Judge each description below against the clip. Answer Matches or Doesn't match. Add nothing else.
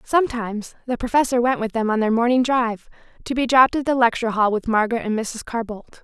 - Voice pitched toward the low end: Doesn't match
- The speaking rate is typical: Doesn't match